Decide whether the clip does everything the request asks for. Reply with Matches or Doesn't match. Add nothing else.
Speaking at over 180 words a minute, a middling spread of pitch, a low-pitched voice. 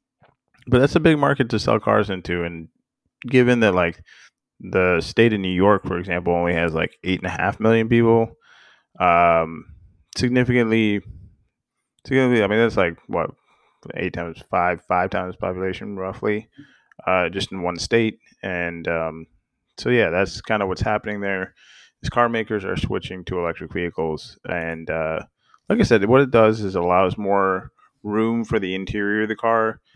Doesn't match